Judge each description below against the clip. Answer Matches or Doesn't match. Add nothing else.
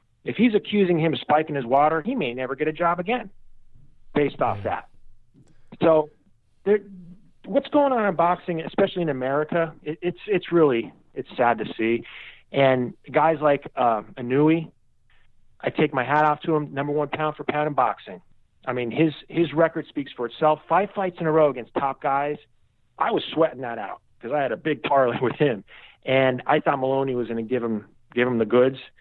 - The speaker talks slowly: Doesn't match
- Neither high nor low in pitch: Matches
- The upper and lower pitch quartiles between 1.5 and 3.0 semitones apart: Doesn't match